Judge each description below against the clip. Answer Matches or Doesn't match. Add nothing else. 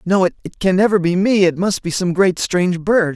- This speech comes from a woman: Doesn't match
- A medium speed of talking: Doesn't match